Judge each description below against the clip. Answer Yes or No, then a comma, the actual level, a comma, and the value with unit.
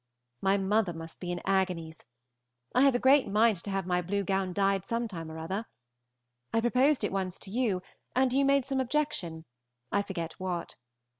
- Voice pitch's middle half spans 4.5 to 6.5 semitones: Yes, average, 5.2 semitones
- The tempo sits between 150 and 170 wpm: No, average, 190 wpm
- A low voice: No, high, 195 Hz